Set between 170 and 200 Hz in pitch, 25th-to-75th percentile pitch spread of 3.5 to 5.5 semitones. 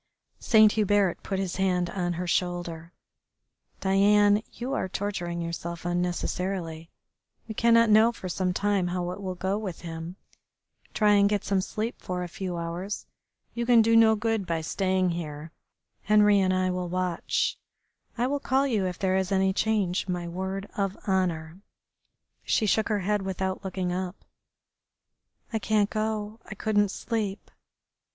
No: high, 190 Hz; average, 2.8 semitones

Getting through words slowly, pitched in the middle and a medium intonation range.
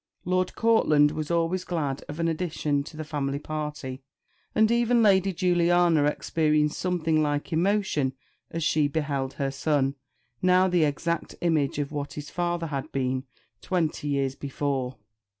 No: average, 150 wpm; medium, 155 Hz; average, 3.4 semitones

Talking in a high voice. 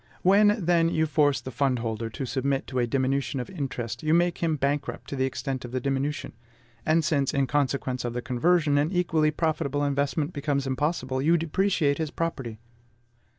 No: medium, 140 Hz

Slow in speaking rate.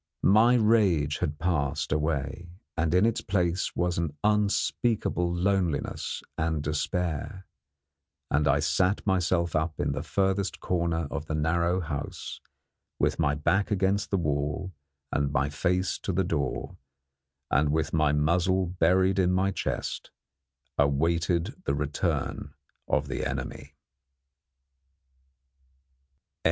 Yes: slow, 120 wpm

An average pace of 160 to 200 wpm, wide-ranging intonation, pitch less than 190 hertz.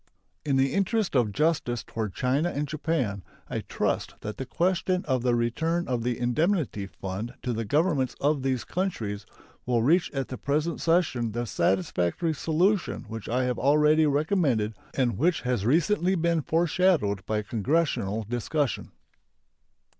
No: average, 150 wpm; wide, 5.9 semitones; low, 135 Hz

